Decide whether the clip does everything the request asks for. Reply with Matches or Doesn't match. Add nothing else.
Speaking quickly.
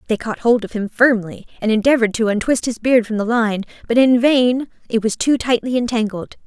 Matches